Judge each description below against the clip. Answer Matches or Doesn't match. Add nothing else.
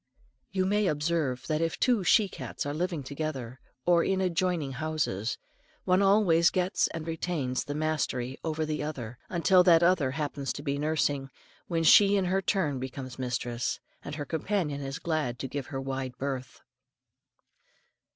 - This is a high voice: Doesn't match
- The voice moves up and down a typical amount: Matches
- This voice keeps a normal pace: Matches